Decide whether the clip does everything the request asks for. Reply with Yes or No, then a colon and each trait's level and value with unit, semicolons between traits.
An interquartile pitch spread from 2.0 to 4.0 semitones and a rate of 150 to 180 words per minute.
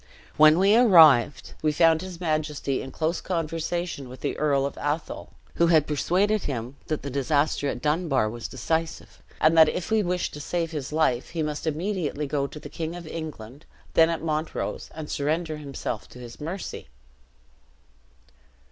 Yes: average, 2.8 semitones; average, 165 wpm